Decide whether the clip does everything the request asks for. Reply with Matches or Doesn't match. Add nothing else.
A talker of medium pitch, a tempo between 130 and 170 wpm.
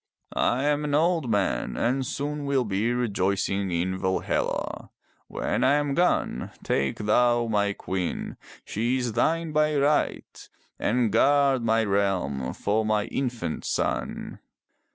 Doesn't match